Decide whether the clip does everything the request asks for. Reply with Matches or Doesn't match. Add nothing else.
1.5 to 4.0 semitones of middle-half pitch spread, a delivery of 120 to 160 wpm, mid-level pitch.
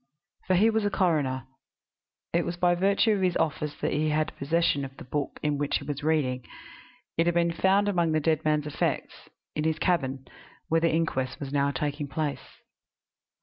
Doesn't match